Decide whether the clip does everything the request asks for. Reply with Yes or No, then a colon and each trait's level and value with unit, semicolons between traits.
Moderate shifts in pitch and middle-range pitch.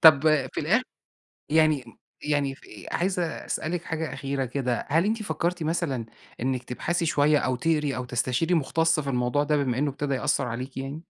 Yes: average, 3.7 semitones; medium, 145 Hz